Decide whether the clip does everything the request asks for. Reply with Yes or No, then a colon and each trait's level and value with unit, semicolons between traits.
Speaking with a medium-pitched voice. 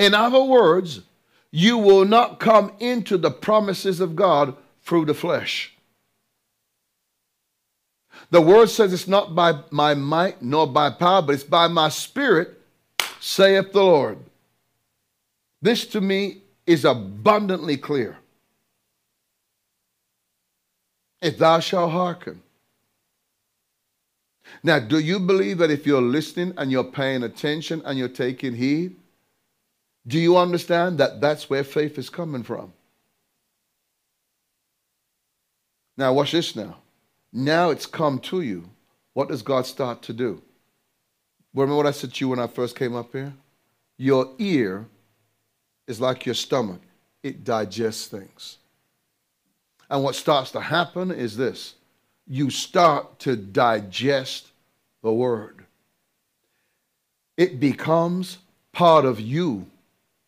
Yes: medium, 150 Hz